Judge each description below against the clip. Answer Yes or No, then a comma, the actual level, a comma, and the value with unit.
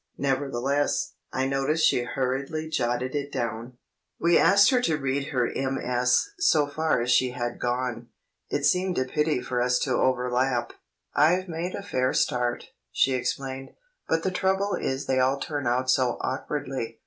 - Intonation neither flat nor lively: Yes, average, 3.4 semitones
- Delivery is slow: No, average, 160 wpm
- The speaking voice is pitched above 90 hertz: Yes, low, 135 Hz